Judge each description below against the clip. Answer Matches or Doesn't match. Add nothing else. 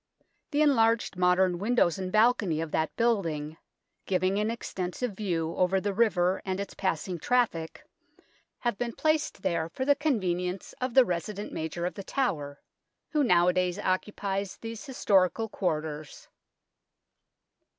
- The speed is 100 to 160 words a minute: Matches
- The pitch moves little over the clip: Doesn't match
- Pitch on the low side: Doesn't match